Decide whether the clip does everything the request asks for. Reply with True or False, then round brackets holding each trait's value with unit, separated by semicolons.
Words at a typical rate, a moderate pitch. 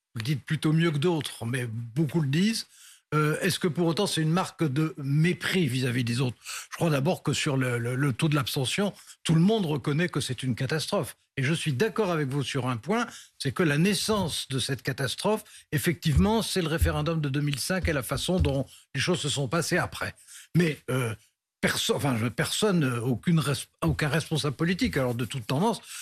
True (195 wpm; 150 Hz)